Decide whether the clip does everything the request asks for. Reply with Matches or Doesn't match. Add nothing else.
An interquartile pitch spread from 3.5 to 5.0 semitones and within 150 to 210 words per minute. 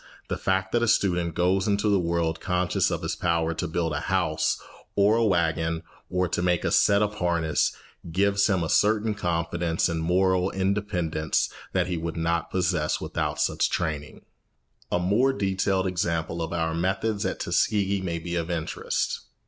Doesn't match